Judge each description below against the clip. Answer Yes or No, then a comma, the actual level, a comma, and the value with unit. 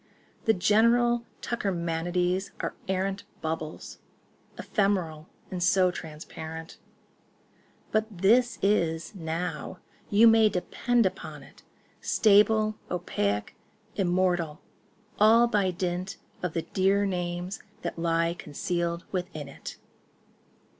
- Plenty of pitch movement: No, average, 3.6 semitones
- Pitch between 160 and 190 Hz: Yes, medium, 185 Hz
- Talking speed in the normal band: No, slow, 90 wpm